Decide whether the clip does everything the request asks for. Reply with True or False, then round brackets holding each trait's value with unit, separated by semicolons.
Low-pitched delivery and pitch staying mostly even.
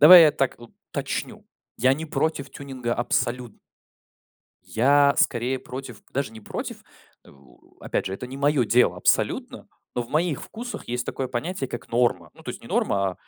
False (130 Hz; 3.2 semitones)